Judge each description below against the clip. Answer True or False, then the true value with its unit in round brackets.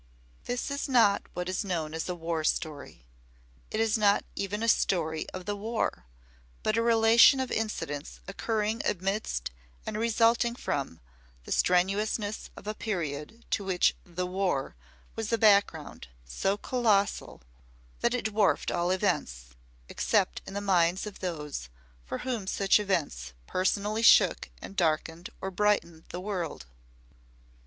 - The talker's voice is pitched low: False (195 Hz)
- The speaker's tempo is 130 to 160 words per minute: True (145 wpm)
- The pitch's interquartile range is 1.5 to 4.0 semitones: False (4.6 semitones)